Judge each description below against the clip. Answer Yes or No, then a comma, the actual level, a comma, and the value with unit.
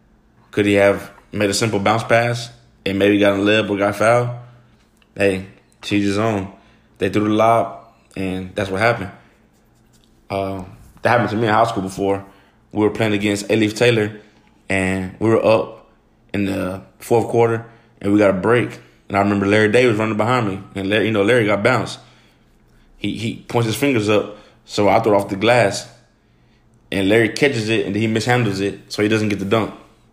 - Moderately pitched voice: No, low, 105 Hz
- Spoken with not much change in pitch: Yes, narrow, 2.3 semitones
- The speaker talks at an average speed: Yes, average, 195 wpm